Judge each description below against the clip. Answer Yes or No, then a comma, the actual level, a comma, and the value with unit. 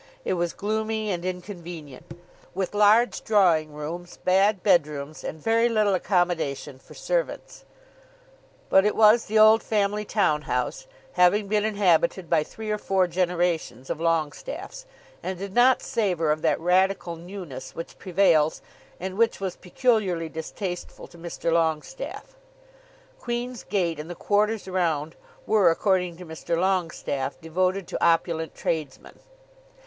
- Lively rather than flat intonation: No, average, 4.2 semitones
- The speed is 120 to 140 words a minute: Yes, slow, 135 wpm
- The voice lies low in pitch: No, medium, 180 Hz